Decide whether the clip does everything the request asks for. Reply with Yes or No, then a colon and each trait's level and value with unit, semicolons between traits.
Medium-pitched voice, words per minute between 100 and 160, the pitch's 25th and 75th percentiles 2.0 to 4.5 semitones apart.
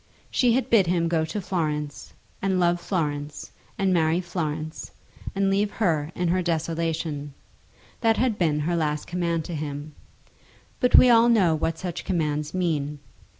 Yes: medium, 170 Hz; average, 155 wpm; average, 3.4 semitones